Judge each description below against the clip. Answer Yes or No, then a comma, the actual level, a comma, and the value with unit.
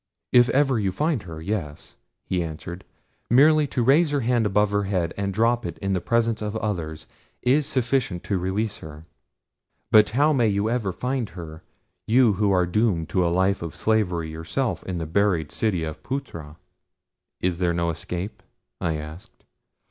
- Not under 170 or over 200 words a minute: Yes, average, 175 wpm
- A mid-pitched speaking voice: No, low, 100 Hz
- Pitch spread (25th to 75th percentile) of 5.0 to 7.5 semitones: Yes, wide, 5.6 semitones